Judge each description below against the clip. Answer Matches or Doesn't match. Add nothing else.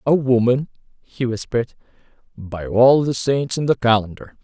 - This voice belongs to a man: Matches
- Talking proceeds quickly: Doesn't match